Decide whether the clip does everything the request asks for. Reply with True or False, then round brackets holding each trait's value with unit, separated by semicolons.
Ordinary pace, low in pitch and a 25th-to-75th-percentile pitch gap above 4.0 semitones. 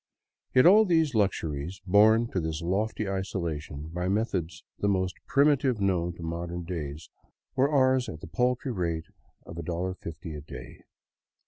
True (145 wpm; 90 Hz; 5.4 semitones)